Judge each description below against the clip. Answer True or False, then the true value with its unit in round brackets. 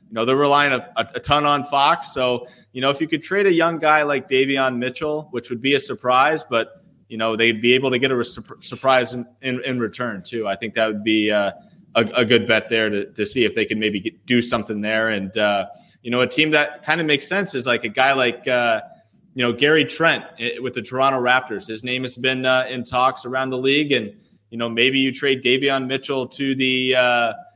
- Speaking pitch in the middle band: False (130 Hz)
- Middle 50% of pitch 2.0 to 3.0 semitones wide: True (2.7 semitones)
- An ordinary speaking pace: False (240 wpm)